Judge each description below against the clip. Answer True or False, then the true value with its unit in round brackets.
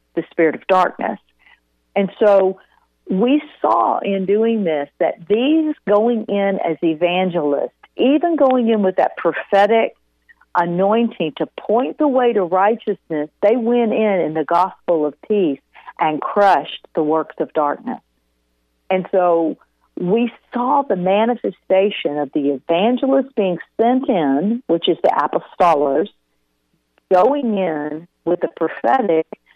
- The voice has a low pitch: False (190 Hz)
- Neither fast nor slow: False (130 wpm)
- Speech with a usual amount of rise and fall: False (5.9 semitones)